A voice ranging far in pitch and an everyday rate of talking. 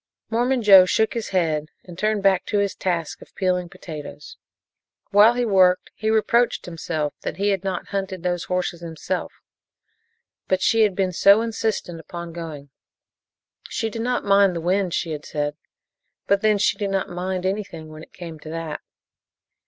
No: average, 3.5 semitones; average, 175 wpm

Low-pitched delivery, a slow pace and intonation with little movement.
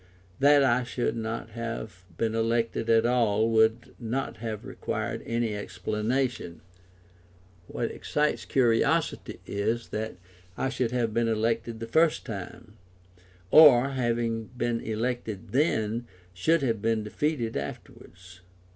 Yes: low, 115 Hz; slow, 120 wpm; narrow, 2.0 semitones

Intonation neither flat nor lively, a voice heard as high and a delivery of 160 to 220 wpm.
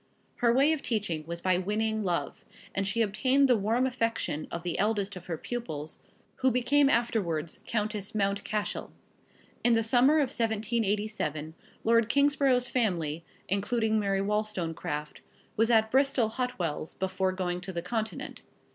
No: average, 4.3 semitones; high, 215 Hz; average, 150 wpm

